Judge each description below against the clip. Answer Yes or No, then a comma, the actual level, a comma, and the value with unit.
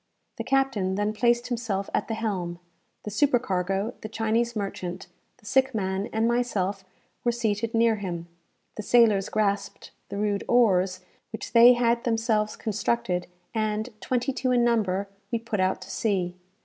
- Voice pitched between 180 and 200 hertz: No, high, 215 Hz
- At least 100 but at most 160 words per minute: Yes, average, 155 wpm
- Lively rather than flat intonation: No, average, 3.3 semitones